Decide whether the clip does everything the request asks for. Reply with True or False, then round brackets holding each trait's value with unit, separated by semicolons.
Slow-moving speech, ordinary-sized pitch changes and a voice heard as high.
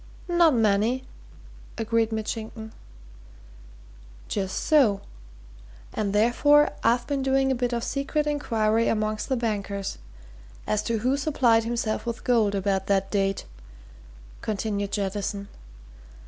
True (115 wpm; 3.7 semitones; 225 Hz)